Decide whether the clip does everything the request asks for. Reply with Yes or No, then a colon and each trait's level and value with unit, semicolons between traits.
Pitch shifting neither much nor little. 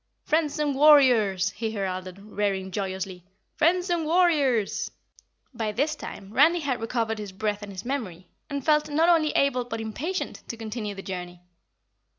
No: wide, 7.1 semitones